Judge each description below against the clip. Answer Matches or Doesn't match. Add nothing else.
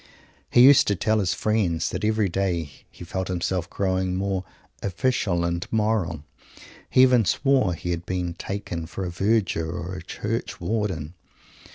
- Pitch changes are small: Doesn't match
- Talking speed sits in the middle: Matches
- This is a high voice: Doesn't match